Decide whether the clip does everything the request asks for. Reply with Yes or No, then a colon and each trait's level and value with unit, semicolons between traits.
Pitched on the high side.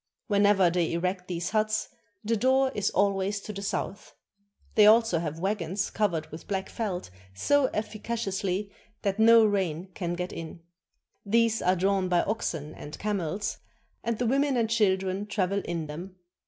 Yes: high, 200 Hz